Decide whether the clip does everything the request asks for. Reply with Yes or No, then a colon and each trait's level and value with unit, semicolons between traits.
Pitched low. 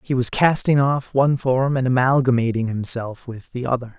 Yes: low, 130 Hz